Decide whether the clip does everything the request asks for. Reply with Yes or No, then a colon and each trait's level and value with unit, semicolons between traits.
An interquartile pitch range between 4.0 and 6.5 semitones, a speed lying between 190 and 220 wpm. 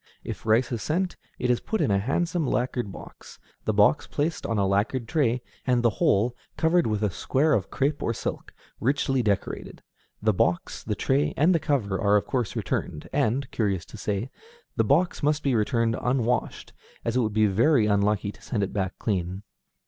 Yes: average, 5.0 semitones; average, 195 wpm